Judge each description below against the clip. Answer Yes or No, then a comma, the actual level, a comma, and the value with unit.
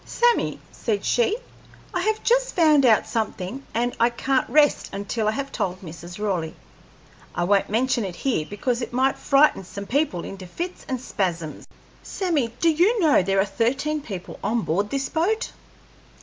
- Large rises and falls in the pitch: Yes, wide, 7.4 semitones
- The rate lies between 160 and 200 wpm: Yes, average, 170 wpm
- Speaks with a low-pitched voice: No, high, 240 Hz